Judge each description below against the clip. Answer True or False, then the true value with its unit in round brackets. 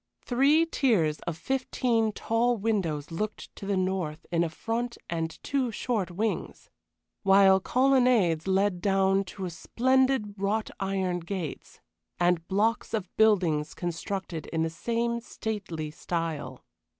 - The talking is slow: True (125 wpm)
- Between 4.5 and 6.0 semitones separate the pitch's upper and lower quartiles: True (5.0 semitones)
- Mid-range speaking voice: False (195 Hz)